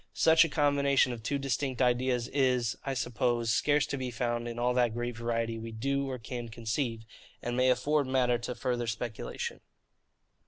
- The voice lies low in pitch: Yes, low, 125 Hz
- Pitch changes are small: Yes, narrow, 2.3 semitones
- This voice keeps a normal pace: Yes, average, 180 wpm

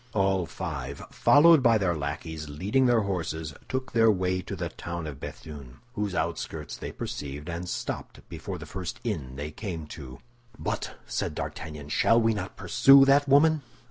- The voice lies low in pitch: Yes, very low, 90 Hz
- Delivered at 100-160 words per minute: No, average, 170 wpm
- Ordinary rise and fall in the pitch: No, wide, 7.0 semitones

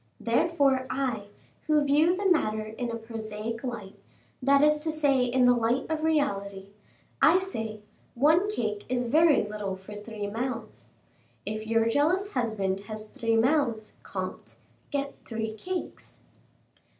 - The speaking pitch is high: Yes, high, 240 Hz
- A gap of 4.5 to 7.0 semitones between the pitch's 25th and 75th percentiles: Yes, average, 5.2 semitones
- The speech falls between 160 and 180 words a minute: No, average, 140 wpm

